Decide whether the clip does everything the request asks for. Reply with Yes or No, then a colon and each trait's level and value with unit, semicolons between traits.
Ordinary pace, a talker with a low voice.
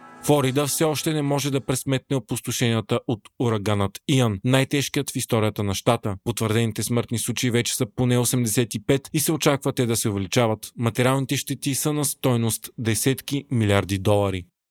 Yes: average, 155 wpm; low, 125 Hz